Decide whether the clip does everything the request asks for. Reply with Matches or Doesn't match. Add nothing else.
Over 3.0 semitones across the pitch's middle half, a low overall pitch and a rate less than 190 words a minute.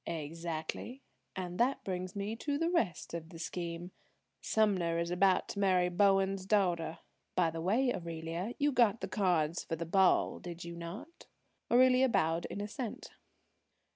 Doesn't match